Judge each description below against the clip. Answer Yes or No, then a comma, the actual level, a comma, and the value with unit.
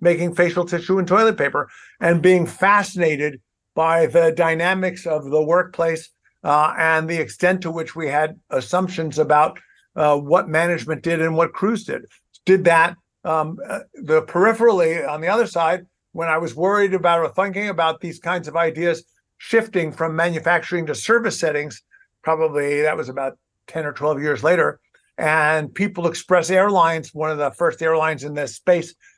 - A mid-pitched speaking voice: Yes, medium, 165 Hz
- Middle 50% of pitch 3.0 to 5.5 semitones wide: No, narrow, 2.6 semitones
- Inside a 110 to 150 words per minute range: No, average, 165 wpm